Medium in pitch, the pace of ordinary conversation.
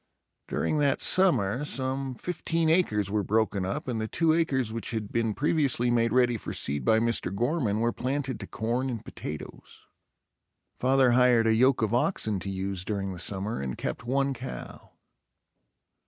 No: low, 120 Hz; average, 170 wpm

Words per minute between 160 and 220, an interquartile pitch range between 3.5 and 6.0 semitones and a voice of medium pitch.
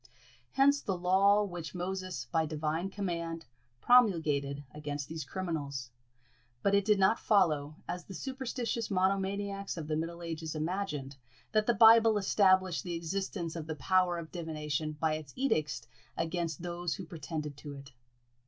No: average, 150 wpm; average, 4.1 semitones; medium, 175 Hz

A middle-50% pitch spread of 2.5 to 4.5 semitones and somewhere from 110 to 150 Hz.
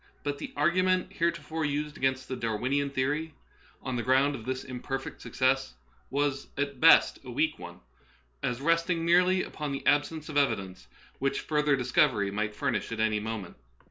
Yes: average, 3.5 semitones; medium, 140 Hz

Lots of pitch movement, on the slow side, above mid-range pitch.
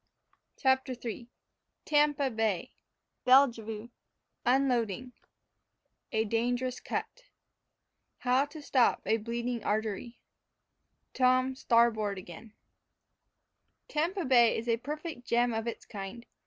No: average, 2.8 semitones; slow, 100 wpm; high, 240 Hz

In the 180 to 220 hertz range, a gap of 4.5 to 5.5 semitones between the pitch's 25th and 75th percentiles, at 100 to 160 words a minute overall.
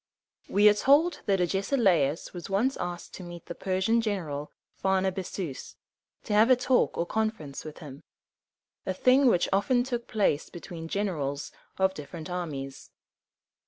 Yes: high, 190 Hz; average, 4.8 semitones; average, 155 wpm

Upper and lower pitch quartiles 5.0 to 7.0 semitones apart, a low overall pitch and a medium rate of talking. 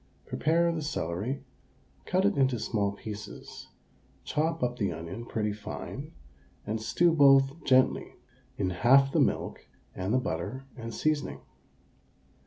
No: wide, 5.6 semitones; low, 125 Hz; slow, 130 wpm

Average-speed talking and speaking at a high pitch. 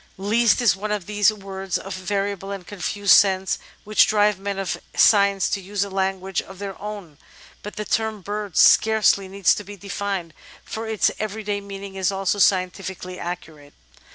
Yes: average, 170 wpm; high, 200 Hz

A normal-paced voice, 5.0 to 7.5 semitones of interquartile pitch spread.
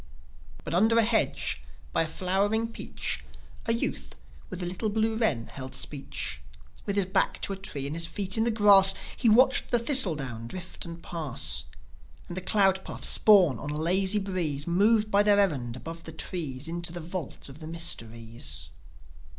Yes: average, 185 wpm; wide, 5.5 semitones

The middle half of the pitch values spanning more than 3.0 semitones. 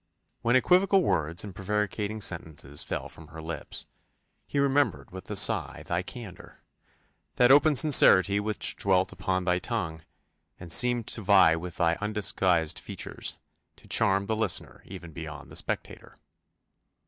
Yes: average, 5.1 semitones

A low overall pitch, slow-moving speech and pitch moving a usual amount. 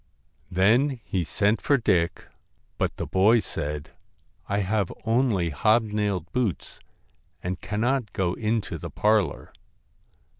Yes: low, 105 Hz; slow, 120 wpm; average, 3.8 semitones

